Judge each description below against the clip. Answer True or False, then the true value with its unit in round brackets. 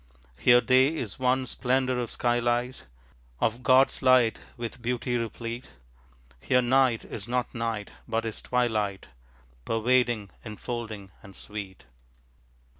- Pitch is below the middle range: True (120 Hz)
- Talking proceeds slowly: True (120 wpm)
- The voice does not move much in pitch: True (2.1 semitones)